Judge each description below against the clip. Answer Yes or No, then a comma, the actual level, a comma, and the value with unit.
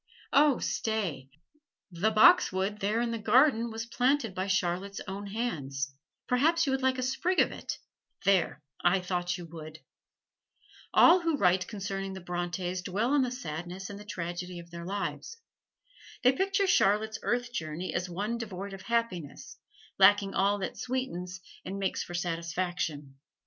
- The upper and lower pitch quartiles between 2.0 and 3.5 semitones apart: No, average, 5.0 semitones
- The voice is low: No, high, 195 Hz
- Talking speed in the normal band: Yes, average, 155 wpm